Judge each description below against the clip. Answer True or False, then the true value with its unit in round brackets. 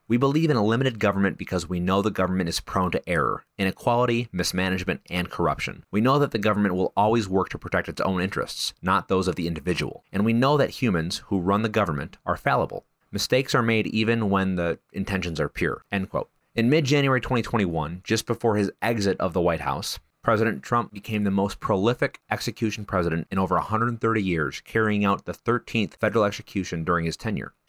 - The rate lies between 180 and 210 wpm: True (200 wpm)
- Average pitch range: True (4.0 semitones)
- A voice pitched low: True (100 Hz)